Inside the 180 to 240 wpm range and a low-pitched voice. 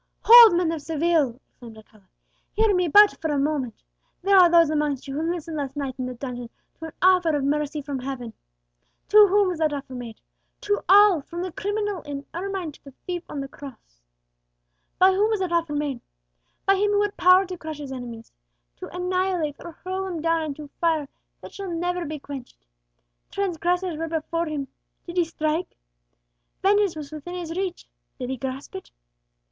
No: average, 190 wpm; very high, 325 Hz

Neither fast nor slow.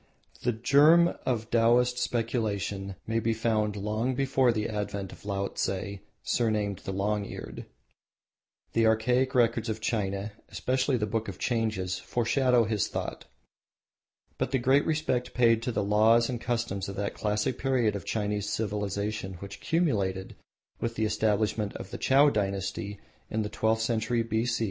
Yes: average, 150 wpm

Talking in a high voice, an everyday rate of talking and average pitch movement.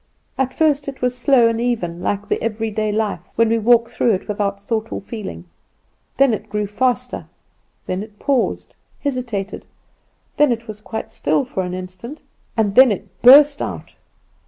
Yes: high, 225 Hz; average, 170 wpm; average, 3.5 semitones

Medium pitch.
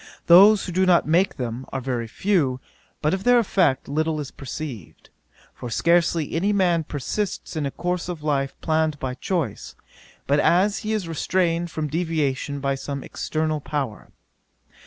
Yes: medium, 155 Hz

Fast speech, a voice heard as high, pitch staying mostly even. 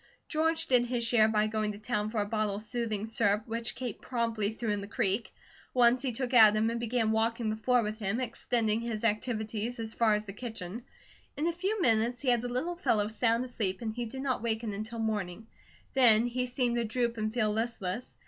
Yes: fast, 215 wpm; high, 230 Hz; narrow, 2.2 semitones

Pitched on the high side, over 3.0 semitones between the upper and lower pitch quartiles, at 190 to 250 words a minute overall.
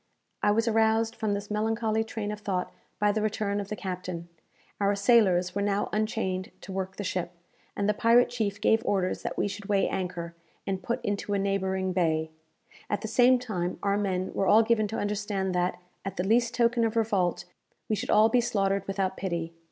No: high, 205 Hz; average, 2.7 semitones; average, 200 wpm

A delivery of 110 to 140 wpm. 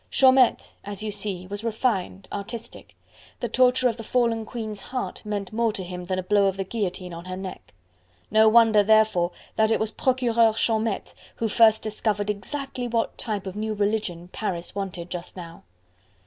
No: average, 175 wpm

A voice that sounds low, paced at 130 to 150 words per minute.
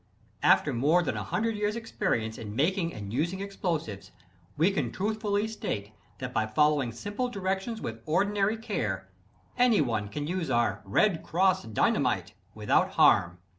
No: medium, 165 Hz; average, 145 wpm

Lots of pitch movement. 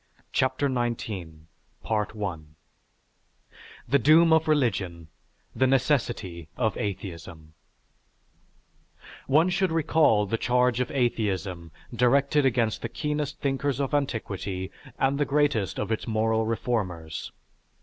Yes: wide, 6.1 semitones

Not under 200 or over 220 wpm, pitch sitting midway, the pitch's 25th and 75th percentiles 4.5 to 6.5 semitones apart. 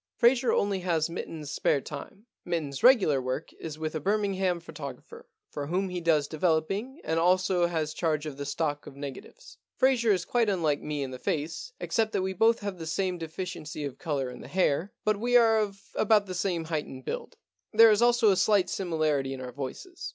Yes: fast, 205 wpm; medium, 175 Hz; average, 5.3 semitones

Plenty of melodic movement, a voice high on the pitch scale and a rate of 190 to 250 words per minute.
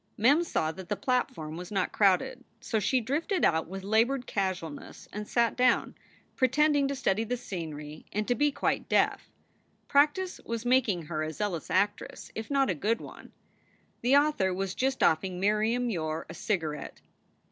No: wide, 6.2 semitones; high, 215 Hz; average, 170 wpm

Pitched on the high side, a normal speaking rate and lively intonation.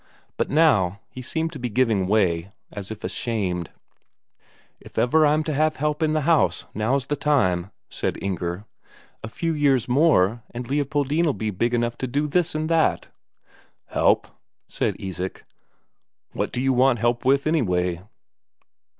No: low, 125 Hz; average, 155 wpm; wide, 6.7 semitones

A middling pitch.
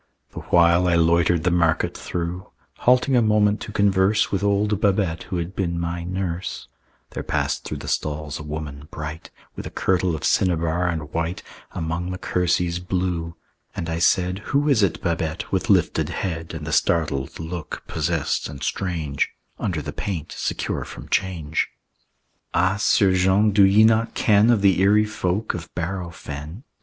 No: very low, 90 Hz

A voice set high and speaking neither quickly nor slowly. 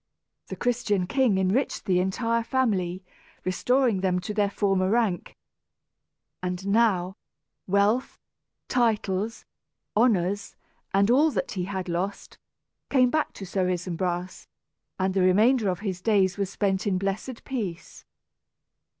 No: high, 195 Hz; slow, 125 wpm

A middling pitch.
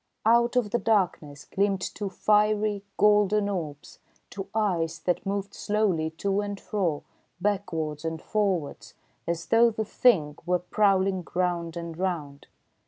No: high, 195 Hz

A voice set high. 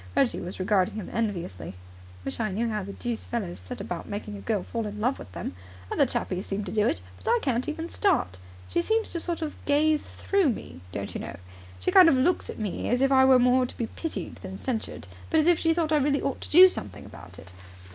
Yes: high, 240 Hz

